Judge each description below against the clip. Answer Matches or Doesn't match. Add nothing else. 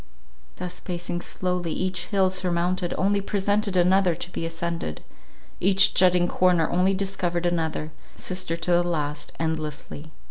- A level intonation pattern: Matches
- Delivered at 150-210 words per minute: Doesn't match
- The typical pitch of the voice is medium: Matches